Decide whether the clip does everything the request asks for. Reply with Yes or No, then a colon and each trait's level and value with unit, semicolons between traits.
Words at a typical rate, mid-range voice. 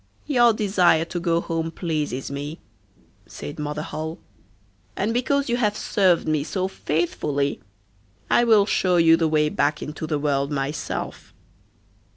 Yes: average, 145 wpm; medium, 165 Hz